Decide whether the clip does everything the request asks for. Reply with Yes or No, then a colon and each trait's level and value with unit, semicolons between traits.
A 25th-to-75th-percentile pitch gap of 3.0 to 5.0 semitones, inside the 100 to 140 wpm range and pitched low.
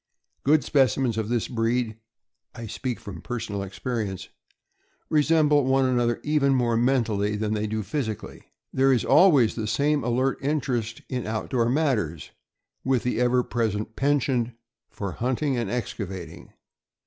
Yes: average, 3.6 semitones; slow, 135 wpm; low, 120 Hz